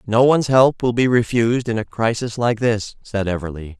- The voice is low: Yes, low, 115 Hz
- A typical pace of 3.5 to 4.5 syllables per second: No, 5.3 syllables/s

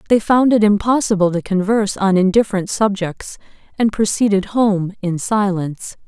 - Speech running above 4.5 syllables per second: Yes, 5.0 syllables/s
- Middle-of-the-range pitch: No, high, 200 Hz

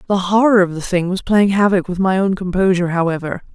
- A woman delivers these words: Yes, female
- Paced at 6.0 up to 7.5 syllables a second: Yes, 6.1 syllables/s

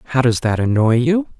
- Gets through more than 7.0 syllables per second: No, 5.5 syllables/s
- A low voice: Yes, low, 125 Hz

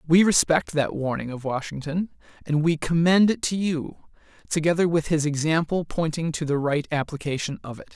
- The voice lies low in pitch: No, medium, 160 Hz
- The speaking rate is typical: Yes, average, 175 wpm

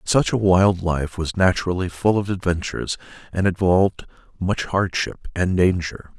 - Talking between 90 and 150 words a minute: Yes, average, 145 wpm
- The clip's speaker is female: No, male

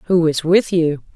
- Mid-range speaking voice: Yes, medium, 165 Hz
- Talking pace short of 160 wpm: No, fast, 205 wpm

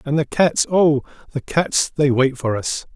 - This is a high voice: No, medium, 145 Hz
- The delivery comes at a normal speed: Yes, average, 180 wpm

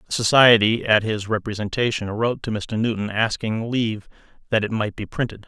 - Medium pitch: No, low, 110 Hz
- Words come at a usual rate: Yes, average, 175 wpm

